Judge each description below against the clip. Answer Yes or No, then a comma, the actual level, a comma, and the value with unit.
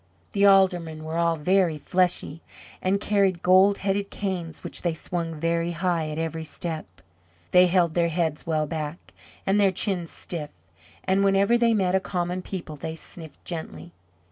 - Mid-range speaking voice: Yes, medium, 175 Hz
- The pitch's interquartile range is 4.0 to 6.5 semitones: No, average, 2.9 semitones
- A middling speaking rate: Yes, average, 160 wpm